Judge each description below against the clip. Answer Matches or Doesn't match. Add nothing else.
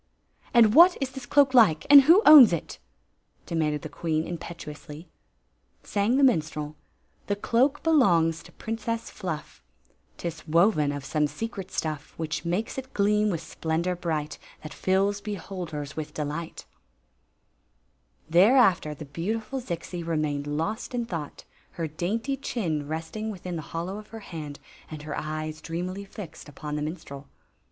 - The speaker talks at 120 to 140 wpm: Doesn't match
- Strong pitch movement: Matches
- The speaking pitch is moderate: Matches